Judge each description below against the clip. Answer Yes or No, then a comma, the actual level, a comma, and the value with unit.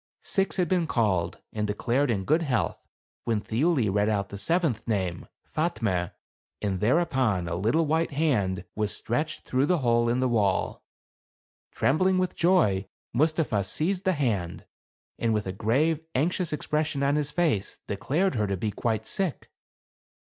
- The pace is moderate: Yes, average, 155 wpm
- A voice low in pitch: Yes, low, 120 Hz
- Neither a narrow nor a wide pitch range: No, wide, 7.5 semitones